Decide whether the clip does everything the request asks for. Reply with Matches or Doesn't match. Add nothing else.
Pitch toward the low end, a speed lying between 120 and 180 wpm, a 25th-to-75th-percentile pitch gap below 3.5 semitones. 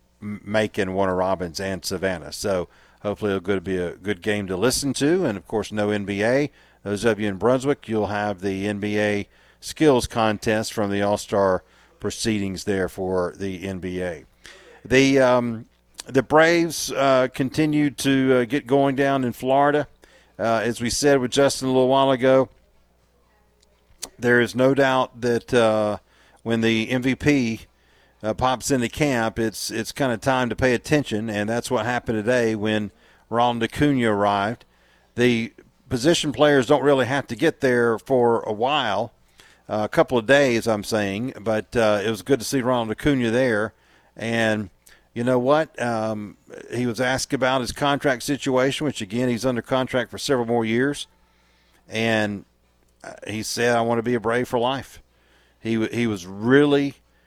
Doesn't match